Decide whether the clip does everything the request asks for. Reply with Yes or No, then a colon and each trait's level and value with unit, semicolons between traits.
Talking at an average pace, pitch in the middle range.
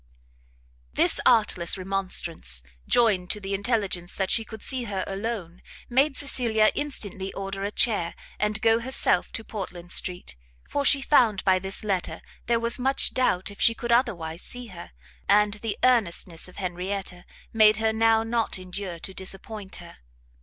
No: average, 160 wpm; high, 205 Hz